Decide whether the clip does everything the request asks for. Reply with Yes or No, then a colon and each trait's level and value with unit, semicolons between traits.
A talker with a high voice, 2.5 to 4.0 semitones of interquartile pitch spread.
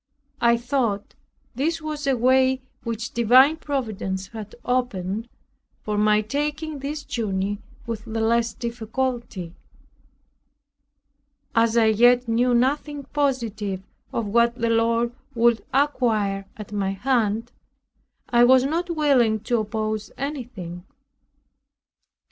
Yes: high, 235 Hz; average, 3.4 semitones